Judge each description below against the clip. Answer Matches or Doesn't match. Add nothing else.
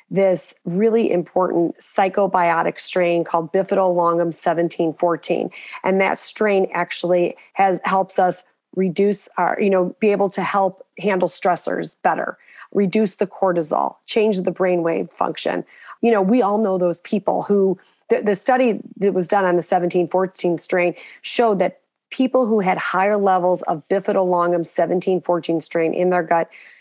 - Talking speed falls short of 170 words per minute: Matches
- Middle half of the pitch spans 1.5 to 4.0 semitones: Matches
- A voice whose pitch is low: Doesn't match